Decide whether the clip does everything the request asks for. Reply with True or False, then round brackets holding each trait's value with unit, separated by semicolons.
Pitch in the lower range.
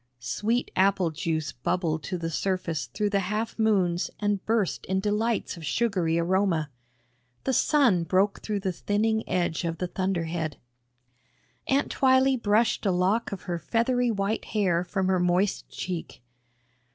False (190 Hz)